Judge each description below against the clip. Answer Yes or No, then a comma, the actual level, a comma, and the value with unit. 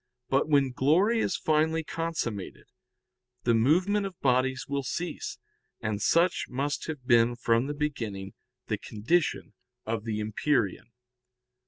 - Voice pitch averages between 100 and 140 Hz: Yes, low, 135 Hz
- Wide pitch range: Yes, wide, 5.8 semitones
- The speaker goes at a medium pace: No, slow, 130 wpm